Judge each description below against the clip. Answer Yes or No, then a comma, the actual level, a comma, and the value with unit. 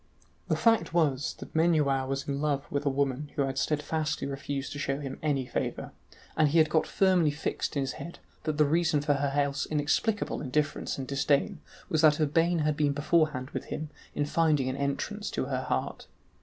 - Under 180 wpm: No, average, 195 wpm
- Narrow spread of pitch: Yes, narrow, 2.2 semitones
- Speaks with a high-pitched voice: No, medium, 145 Hz